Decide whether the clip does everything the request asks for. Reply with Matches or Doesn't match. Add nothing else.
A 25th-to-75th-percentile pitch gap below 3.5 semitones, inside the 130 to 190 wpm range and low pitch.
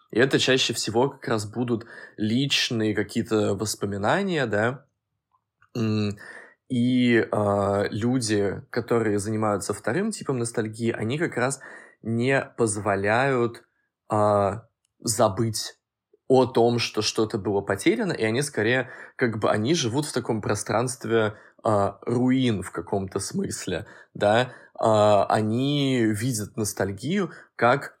Doesn't match